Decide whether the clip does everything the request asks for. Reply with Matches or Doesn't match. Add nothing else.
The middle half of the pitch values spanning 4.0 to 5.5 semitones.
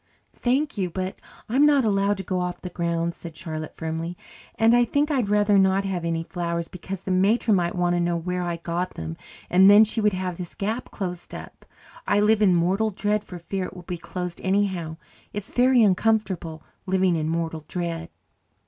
Doesn't match